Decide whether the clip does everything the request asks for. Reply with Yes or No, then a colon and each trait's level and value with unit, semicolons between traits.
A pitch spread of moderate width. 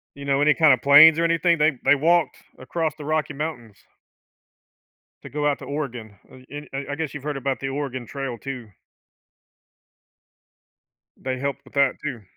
No: narrow, 2.3 semitones